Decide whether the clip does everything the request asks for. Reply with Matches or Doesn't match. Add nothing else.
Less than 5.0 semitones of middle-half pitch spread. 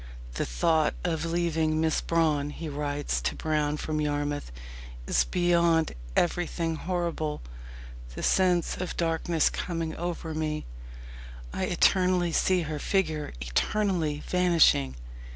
Matches